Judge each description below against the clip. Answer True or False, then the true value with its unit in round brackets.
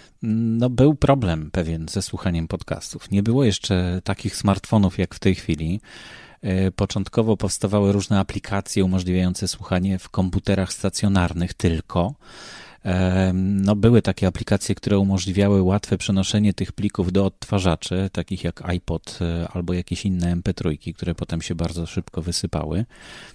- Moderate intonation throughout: False (2.3 semitones)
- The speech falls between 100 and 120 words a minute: False (130 wpm)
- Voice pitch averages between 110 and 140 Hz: False (95 Hz)